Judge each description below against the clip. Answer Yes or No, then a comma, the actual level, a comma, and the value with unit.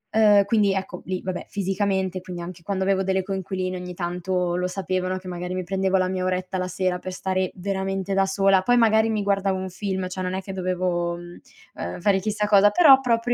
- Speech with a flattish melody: Yes, narrow, 1.3 semitones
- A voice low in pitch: No, high, 190 Hz